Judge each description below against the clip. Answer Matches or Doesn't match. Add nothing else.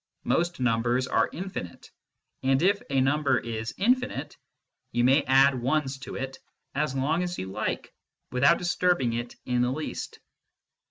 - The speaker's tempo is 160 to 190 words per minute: Doesn't match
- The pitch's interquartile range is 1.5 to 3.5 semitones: Doesn't match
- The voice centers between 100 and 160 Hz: Matches